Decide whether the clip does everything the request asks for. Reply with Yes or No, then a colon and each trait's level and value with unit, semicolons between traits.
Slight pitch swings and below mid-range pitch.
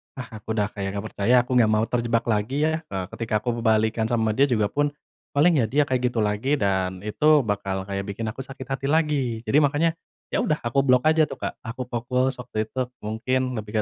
No: average, 4.0 semitones; low, 115 Hz